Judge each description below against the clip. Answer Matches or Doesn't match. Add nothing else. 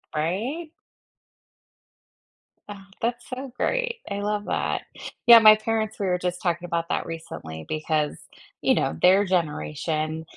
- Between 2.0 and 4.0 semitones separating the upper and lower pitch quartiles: Doesn't match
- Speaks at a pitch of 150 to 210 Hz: Matches